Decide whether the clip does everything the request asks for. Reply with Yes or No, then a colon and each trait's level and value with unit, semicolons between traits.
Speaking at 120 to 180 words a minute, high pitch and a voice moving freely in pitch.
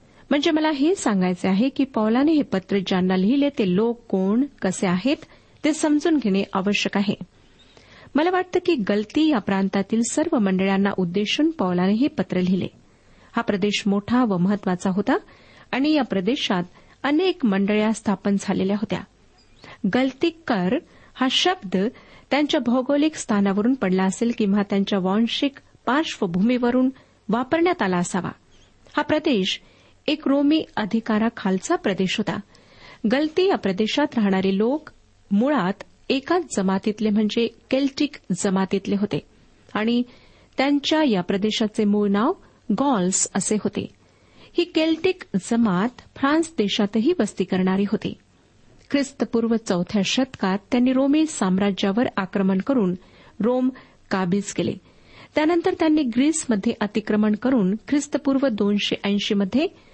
Yes: average, 125 wpm; high, 220 Hz; wide, 6.0 semitones